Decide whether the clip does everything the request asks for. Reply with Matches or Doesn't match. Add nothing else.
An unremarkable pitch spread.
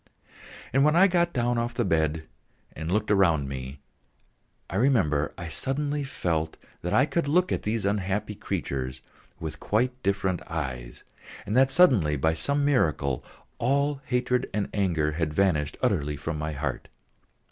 Doesn't match